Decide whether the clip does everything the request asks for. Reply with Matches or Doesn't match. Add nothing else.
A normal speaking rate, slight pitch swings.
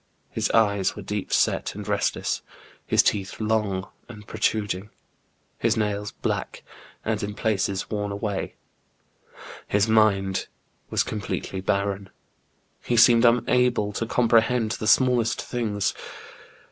Doesn't match